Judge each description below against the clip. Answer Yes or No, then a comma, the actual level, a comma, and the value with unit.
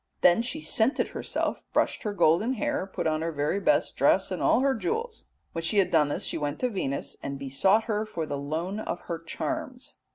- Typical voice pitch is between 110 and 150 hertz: No, high, 190 Hz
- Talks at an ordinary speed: No, fast, 215 wpm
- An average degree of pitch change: No, wide, 7.3 semitones